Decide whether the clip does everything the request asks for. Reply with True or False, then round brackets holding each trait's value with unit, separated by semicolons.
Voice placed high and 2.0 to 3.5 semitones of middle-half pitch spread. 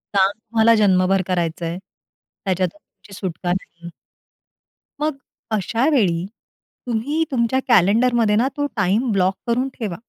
False (210 Hz; 4.4 semitones)